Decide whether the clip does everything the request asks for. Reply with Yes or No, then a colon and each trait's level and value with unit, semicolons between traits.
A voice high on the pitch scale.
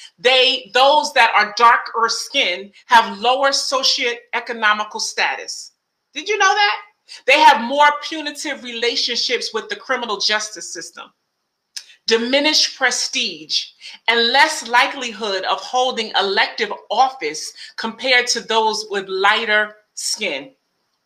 Yes: high, 245 Hz